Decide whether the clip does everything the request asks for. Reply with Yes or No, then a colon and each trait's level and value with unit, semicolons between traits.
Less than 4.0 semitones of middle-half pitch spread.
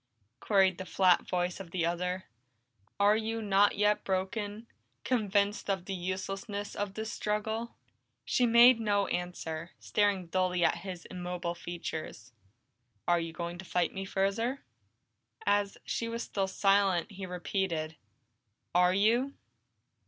Yes: average, 2.7 semitones